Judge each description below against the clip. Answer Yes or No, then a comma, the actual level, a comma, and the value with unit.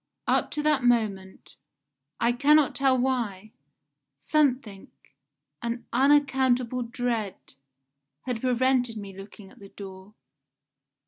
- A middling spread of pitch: Yes, average, 4.1 semitones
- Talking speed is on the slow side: Yes, slow, 105 wpm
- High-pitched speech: Yes, high, 245 Hz